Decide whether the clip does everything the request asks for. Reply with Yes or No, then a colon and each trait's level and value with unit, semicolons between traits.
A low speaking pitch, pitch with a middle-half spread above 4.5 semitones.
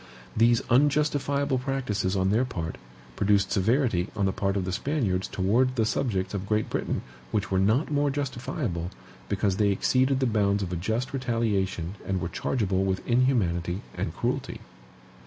Yes: low, 105 Hz; average, 5.2 semitones